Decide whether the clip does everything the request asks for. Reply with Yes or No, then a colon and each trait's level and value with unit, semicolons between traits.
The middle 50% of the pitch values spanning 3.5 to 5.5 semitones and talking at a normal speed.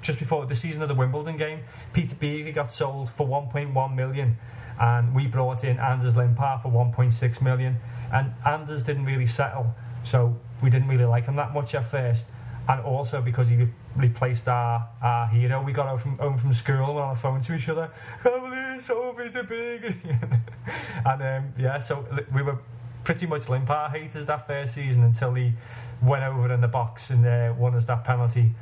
No: average, 3.1 semitones; average, 195 wpm